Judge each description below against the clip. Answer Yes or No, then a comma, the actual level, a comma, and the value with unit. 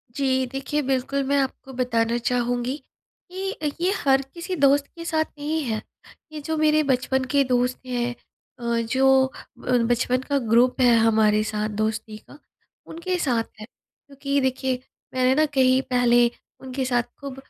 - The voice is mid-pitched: No, very high, 260 Hz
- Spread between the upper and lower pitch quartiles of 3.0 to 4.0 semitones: No, narrow, 2.6 semitones